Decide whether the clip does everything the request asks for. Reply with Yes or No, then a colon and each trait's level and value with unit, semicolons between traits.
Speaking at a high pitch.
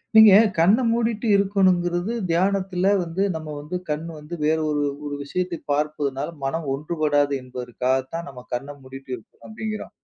No: medium, 160 Hz